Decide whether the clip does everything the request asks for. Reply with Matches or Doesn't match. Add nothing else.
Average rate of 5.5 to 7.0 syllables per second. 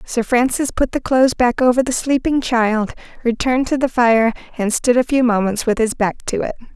Doesn't match